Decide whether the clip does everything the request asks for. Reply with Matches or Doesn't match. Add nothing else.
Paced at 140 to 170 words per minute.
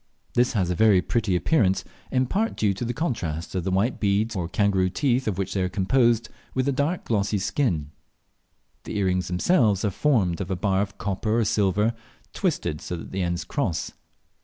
Doesn't match